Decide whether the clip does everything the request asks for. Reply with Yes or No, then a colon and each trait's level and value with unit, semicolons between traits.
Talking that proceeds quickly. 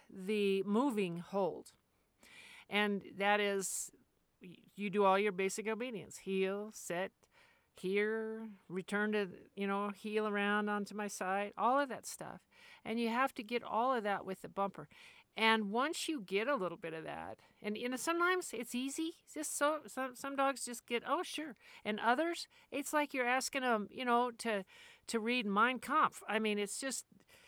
No: average, 180 wpm